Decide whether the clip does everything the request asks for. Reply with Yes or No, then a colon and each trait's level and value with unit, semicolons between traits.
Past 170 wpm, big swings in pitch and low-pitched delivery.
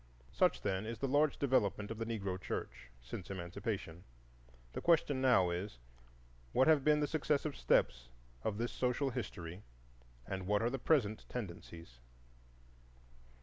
No: average, 145 wpm; wide, 6.4 semitones; low, 110 Hz